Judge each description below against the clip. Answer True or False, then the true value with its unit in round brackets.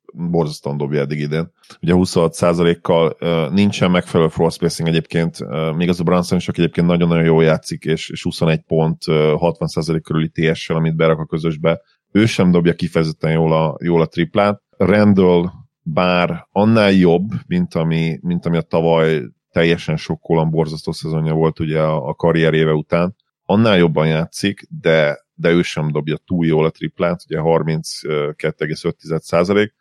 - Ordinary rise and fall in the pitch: False (1.5 semitones)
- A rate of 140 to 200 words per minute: True (150 wpm)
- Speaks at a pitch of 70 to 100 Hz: True (80 Hz)